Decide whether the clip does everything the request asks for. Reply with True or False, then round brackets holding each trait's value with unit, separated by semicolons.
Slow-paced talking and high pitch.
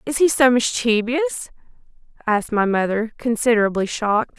True (125 wpm; 225 Hz)